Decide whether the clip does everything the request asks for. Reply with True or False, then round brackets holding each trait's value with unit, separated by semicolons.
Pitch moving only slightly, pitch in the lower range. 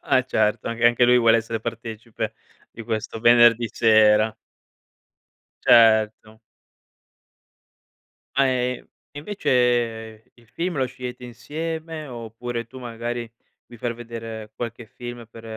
True (1.6 semitones; 120 Hz)